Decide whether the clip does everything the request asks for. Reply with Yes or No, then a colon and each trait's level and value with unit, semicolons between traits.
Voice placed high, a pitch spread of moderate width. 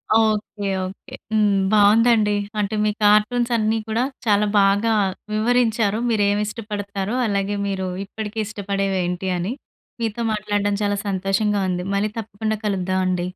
No: high, 205 Hz; narrow, 1.7 semitones